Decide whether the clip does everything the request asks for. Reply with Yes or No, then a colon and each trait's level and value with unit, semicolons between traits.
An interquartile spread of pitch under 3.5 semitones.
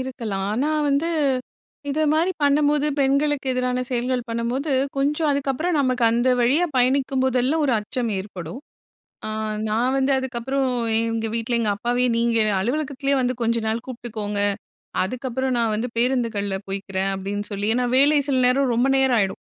Yes: average, 3.0 semitones